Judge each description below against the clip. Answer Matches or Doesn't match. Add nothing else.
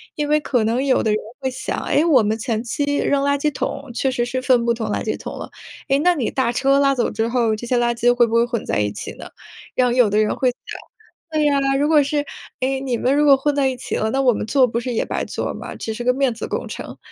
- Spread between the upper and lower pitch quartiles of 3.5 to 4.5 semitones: Doesn't match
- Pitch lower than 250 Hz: Doesn't match